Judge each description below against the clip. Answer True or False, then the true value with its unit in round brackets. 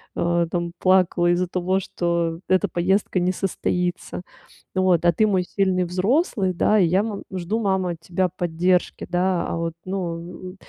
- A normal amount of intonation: False (1.5 semitones)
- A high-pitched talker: False (180 Hz)